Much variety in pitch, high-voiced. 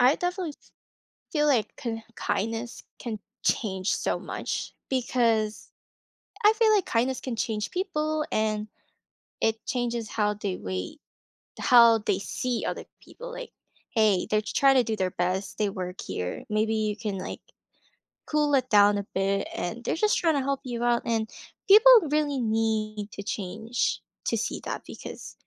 No: average, 4.2 semitones; high, 225 Hz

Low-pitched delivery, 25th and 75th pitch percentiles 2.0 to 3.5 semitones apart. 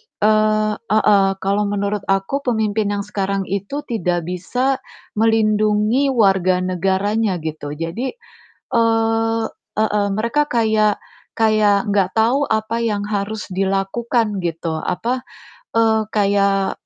No: high, 210 Hz; narrow, 2.6 semitones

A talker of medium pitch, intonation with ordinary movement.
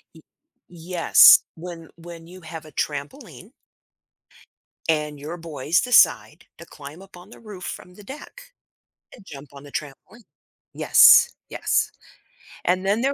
Yes: medium, 170 Hz; average, 4.1 semitones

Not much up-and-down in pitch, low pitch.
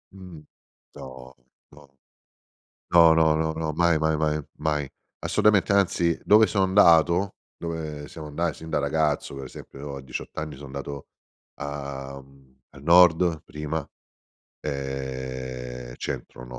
No: average, 3.2 semitones; very low, 75 Hz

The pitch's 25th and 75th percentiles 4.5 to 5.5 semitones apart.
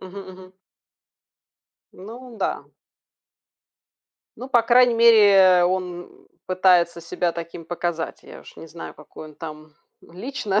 Yes: average, 5.0 semitones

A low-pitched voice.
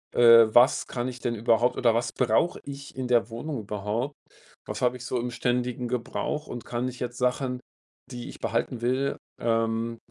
Yes: low, 120 Hz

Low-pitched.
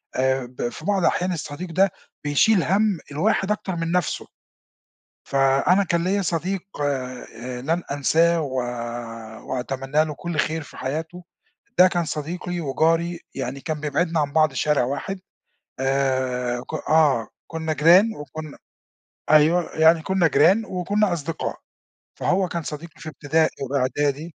No: medium, 160 Hz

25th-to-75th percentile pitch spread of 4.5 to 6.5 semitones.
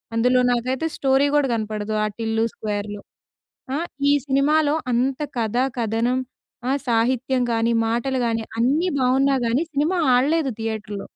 No: average, 3.2 semitones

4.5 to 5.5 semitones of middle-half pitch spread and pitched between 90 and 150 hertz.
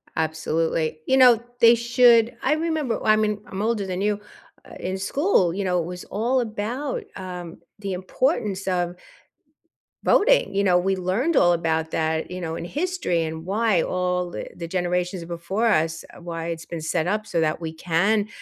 No: average, 4.8 semitones; medium, 185 Hz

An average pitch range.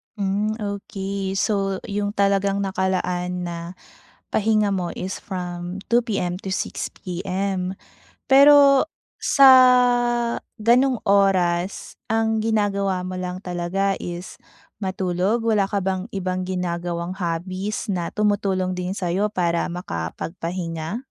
No: narrow, 2.2 semitones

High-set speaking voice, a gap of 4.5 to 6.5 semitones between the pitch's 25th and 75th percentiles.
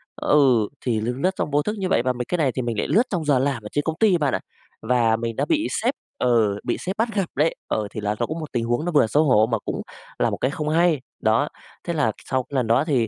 No: low, 135 Hz; wide, 5.5 semitones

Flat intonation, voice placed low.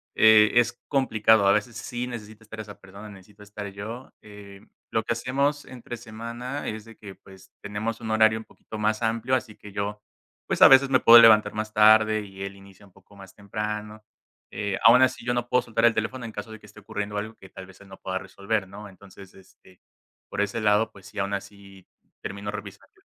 Yes: narrow, 2.2 semitones; low, 105 Hz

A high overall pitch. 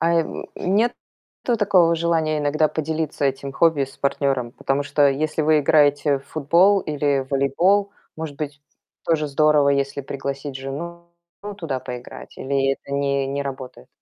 No: medium, 145 Hz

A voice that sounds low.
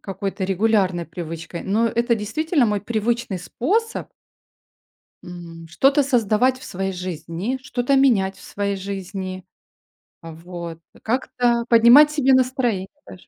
No: high, 210 Hz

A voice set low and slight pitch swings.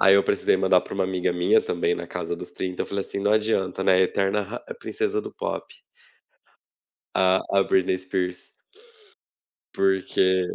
Yes: very low, 95 Hz; narrow, 1.3 semitones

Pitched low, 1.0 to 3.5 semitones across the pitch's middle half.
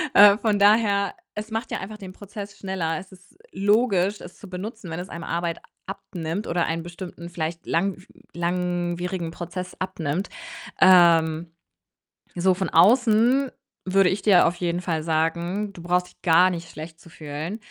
No: medium, 180 Hz; average, 2.8 semitones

